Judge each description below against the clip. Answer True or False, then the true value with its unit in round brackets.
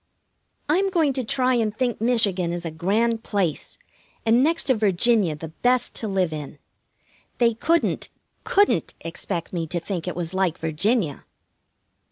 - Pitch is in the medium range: False (210 Hz)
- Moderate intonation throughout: False (6.2 semitones)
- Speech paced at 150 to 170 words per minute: True (155 wpm)